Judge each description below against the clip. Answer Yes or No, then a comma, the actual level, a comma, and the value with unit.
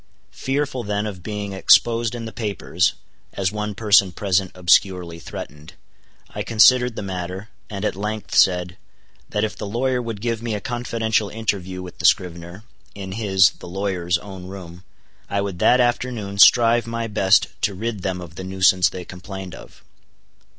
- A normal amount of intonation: Yes, average, 3.5 semitones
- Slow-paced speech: No, average, 165 wpm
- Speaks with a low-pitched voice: Yes, low, 100 Hz